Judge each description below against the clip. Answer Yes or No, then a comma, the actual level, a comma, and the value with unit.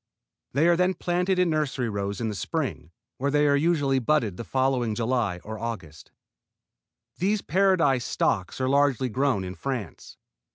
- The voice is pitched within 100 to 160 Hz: Yes, low, 135 Hz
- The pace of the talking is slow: No, average, 160 wpm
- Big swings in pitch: Yes, wide, 5.7 semitones